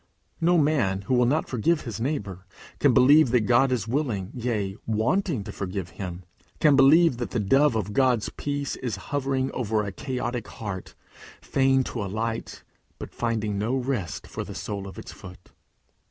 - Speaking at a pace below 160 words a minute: No, average, 170 wpm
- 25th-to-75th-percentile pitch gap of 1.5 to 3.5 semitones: No, average, 4.8 semitones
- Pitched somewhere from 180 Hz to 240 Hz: No, low, 120 Hz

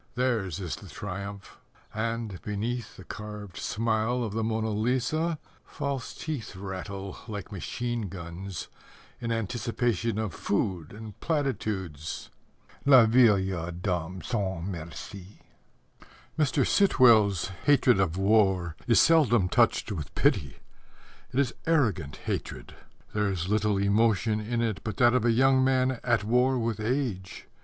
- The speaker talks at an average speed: No, slow, 130 wpm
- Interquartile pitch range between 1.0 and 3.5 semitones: No, average, 4.0 semitones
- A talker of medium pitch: No, low, 110 Hz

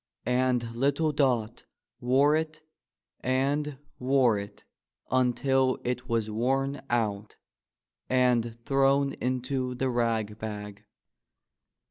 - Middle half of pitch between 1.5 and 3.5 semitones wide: Yes, average, 2.7 semitones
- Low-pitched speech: Yes, low, 125 Hz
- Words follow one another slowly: Yes, slow, 95 wpm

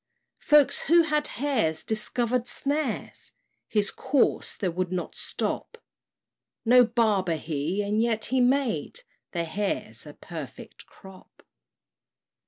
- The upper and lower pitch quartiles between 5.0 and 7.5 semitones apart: Yes, wide, 5.6 semitones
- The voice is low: No, high, 225 Hz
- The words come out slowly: Yes, slow, 115 wpm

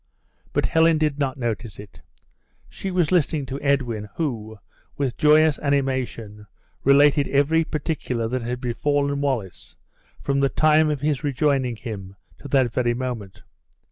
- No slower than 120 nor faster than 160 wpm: Yes, average, 140 wpm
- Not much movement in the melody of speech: No, average, 3.8 semitones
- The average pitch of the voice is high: No, medium, 140 Hz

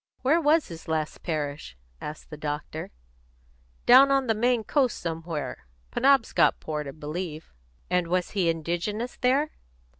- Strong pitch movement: Yes, wide, 8.3 semitones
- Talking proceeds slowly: Yes, slow, 130 wpm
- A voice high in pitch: No, medium, 175 Hz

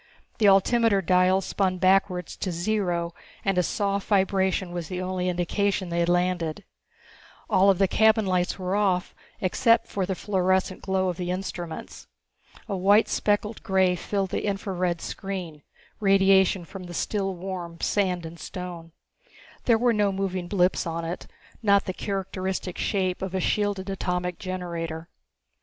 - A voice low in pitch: No, medium, 185 Hz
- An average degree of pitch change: No, narrow, 1.8 semitones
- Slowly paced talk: No, average, 155 wpm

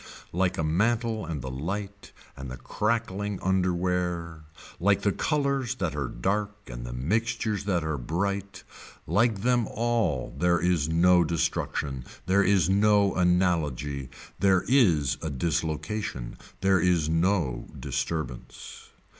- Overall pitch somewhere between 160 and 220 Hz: No, very low, 90 Hz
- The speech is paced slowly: Yes, slow, 130 wpm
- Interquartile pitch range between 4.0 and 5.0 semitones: Yes, average, 4.7 semitones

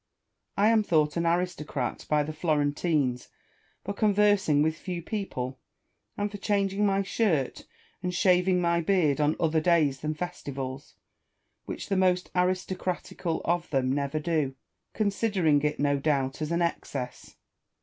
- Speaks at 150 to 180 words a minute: No, average, 140 wpm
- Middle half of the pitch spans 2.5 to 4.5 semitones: Yes, average, 4.2 semitones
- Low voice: No, medium, 170 Hz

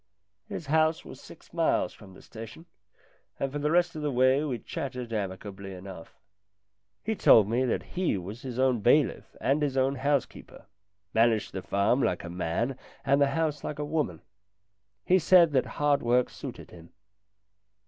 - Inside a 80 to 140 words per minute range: No, average, 170 wpm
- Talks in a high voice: No, low, 130 Hz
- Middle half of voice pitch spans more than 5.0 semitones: Yes, wide, 5.6 semitones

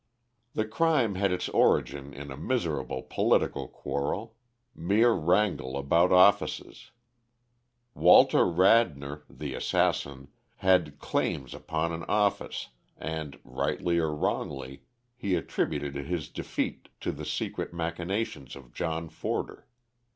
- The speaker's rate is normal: No, slow, 115 wpm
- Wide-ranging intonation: Yes, wide, 5.8 semitones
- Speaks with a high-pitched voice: No, very low, 85 Hz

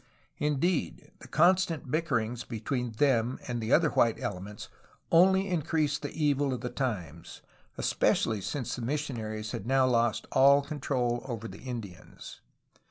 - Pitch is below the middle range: Yes, low, 130 Hz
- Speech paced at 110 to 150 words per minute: Yes, average, 140 wpm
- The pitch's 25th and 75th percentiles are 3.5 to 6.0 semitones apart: Yes, average, 4.5 semitones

